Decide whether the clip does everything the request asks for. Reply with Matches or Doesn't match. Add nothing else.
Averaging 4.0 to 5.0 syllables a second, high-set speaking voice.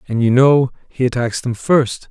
Doesn't match